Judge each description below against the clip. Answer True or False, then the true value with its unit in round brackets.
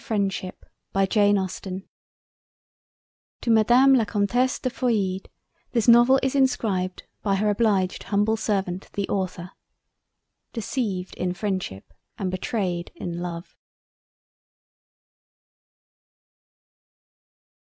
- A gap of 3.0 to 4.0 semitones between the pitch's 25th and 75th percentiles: True (3.7 semitones)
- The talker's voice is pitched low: False (200 Hz)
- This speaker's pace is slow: True (90 wpm)